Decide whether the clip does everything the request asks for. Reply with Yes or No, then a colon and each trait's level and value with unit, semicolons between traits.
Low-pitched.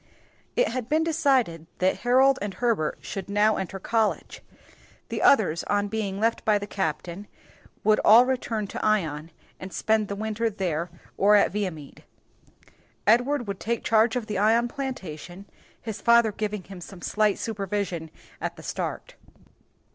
No: high, 210 Hz